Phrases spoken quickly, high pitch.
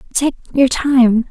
No: average, 140 wpm; very high, 255 Hz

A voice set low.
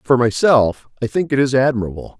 Yes: low, 120 Hz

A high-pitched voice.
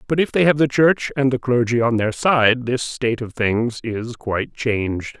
No: low, 125 Hz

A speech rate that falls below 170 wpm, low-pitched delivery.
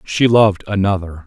Yes: average, 140 wpm; low, 100 Hz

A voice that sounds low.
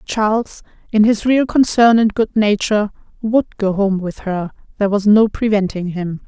No: high, 210 Hz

